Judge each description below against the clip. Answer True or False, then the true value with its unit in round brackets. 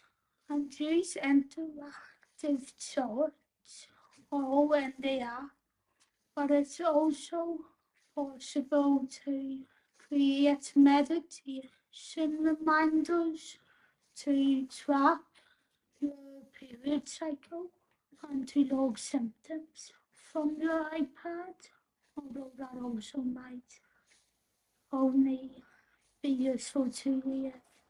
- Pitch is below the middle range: False (285 Hz)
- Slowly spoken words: True (80 wpm)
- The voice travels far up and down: False (2.6 semitones)